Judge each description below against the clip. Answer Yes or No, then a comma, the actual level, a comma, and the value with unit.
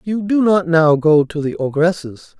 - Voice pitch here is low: No, medium, 170 Hz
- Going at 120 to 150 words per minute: No, average, 200 wpm